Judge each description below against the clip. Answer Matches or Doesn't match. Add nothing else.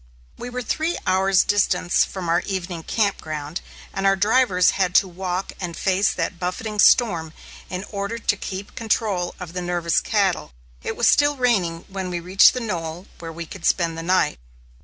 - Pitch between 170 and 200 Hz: Matches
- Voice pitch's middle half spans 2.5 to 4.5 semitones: Matches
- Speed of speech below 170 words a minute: Doesn't match